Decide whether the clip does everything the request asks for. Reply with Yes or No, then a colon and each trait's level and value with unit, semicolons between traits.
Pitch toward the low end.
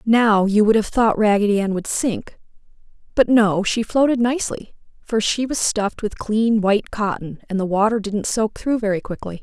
No: high, 215 Hz